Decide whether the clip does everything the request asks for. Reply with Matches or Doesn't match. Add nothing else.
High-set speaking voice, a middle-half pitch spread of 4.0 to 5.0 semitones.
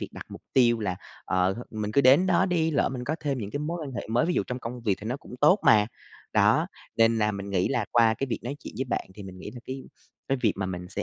Doesn't match